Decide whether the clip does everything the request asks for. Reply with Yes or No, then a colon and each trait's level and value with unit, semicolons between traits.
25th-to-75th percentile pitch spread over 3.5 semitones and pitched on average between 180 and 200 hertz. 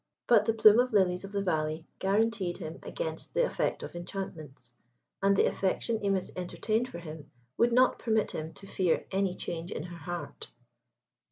Yes: average, 4.4 semitones; high, 190 Hz